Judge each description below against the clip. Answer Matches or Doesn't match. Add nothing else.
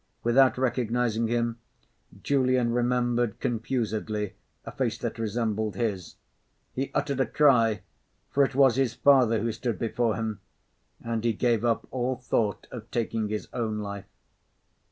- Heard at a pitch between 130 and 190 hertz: Doesn't match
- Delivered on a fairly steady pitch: Matches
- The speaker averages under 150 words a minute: Matches